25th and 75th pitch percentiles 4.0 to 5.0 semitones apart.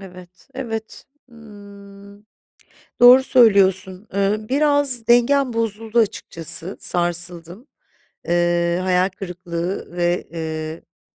Yes: average, 4.5 semitones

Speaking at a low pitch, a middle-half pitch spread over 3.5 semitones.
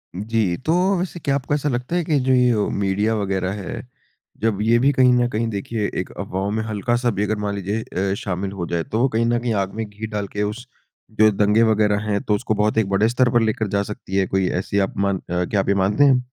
No: low, 105 Hz; average, 3.0 semitones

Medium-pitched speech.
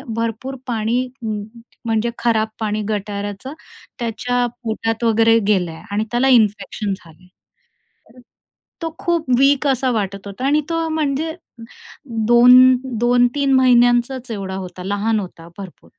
No: high, 230 Hz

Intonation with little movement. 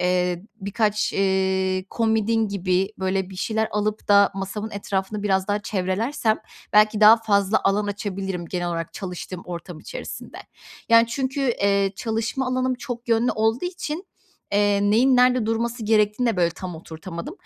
No: average, 3.1 semitones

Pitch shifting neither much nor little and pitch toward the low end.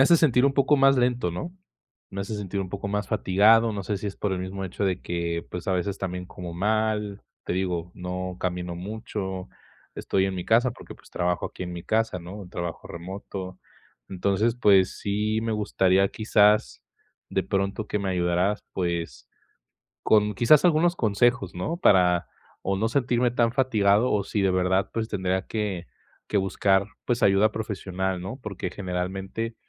Yes: average, 3.1 semitones; low, 100 Hz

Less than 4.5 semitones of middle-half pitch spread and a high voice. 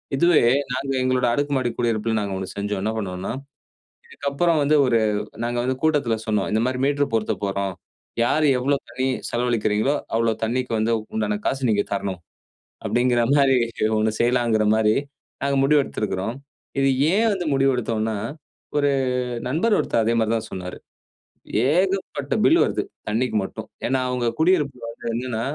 No: average, 4.1 semitones; low, 120 Hz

